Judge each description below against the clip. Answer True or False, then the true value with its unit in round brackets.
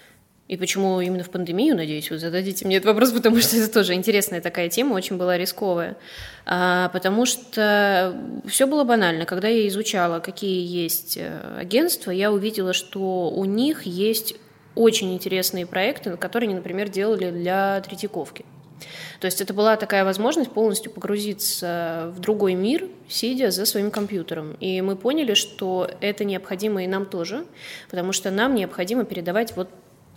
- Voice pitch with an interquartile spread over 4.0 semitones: False (3.2 semitones)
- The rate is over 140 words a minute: True (155 wpm)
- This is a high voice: True (195 Hz)